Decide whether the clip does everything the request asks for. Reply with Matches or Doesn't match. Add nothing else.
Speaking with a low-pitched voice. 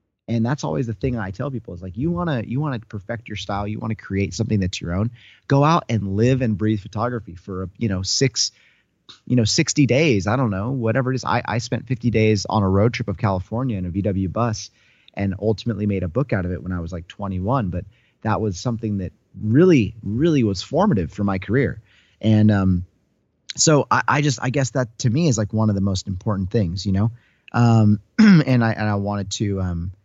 Matches